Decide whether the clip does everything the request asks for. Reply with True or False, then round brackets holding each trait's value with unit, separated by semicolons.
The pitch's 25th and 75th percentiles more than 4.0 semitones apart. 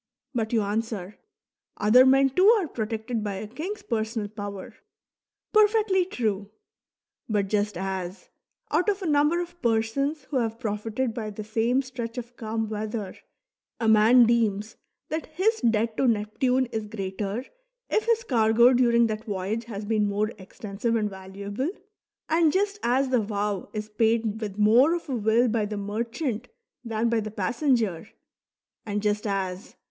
False (3.4 semitones)